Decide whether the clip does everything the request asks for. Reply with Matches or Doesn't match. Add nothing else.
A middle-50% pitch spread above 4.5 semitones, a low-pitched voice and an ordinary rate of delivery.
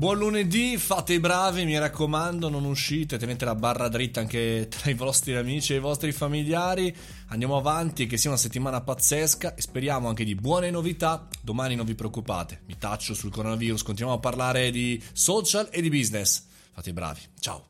Doesn't match